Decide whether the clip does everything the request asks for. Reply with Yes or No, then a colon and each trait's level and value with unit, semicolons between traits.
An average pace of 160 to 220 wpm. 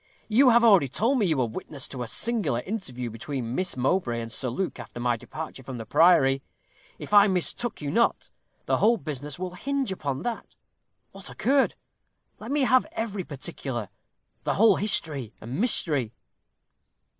Yes: average, 170 wpm